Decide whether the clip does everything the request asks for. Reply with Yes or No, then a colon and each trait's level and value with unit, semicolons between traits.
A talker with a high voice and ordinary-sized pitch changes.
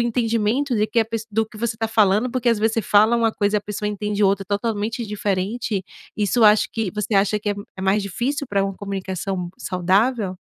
No: high, 210 Hz; narrow, 2.3 semitones